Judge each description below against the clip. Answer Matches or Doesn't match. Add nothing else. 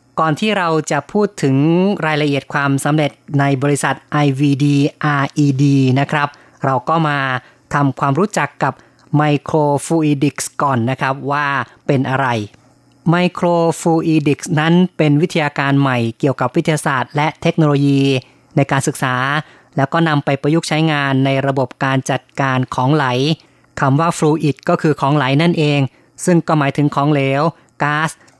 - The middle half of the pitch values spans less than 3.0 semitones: Matches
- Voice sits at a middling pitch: Matches